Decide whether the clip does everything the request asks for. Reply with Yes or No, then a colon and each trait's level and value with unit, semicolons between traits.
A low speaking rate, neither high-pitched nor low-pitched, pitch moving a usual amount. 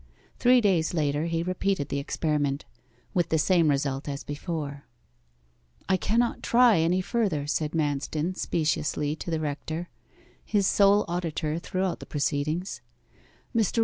Yes: slow, 130 wpm; medium, 160 Hz; average, 3.9 semitones